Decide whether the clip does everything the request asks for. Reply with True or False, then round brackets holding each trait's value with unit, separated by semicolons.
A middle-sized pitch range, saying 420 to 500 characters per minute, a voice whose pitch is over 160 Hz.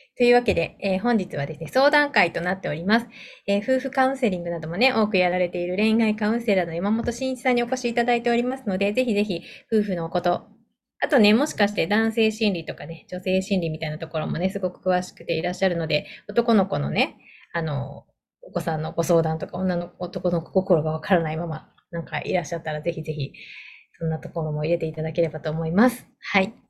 True (5.0 semitones; 450 characters per minute; 185 Hz)